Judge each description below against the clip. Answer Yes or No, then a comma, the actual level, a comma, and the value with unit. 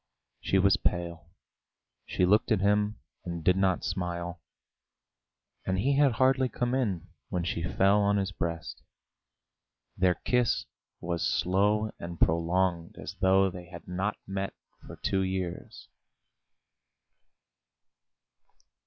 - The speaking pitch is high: No, very low, 95 Hz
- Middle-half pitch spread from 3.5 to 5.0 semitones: No, average, 2.8 semitones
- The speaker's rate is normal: No, slow, 120 wpm